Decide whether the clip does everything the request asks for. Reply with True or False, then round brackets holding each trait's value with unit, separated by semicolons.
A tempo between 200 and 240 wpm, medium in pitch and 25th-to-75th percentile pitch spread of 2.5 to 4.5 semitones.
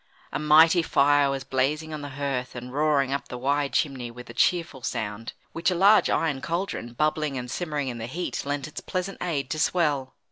True (205 wpm; 145 Hz; 3.3 semitones)